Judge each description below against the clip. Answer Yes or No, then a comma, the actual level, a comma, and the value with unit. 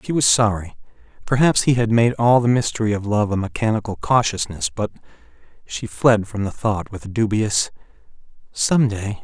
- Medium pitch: No, low, 110 Hz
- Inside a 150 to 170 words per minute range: Yes, average, 155 wpm